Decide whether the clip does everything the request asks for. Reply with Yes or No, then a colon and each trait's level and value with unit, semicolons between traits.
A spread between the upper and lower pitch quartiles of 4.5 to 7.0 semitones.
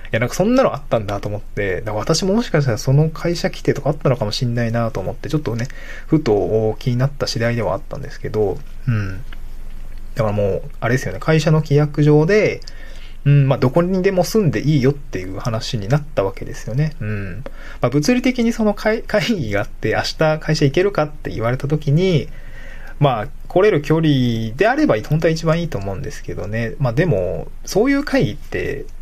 Yes: wide, 5.5 semitones